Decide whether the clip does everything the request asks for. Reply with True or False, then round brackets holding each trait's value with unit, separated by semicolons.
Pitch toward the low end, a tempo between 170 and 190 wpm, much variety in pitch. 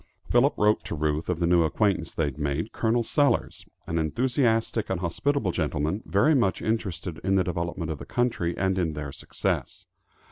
True (90 Hz; 180 wpm; 5.7 semitones)